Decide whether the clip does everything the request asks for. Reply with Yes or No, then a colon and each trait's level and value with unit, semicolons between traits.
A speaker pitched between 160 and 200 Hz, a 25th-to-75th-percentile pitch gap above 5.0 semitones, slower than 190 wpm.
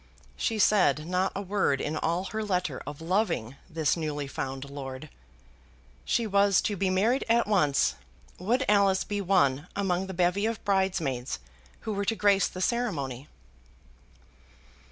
Yes: medium, 185 Hz; wide, 5.5 semitones; average, 150 wpm